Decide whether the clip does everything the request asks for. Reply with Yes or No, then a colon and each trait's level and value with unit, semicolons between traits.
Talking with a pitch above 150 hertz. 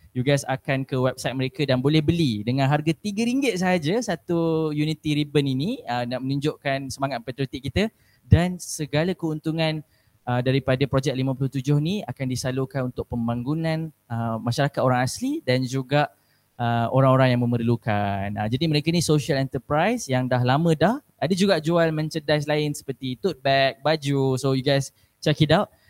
No: medium, 140 Hz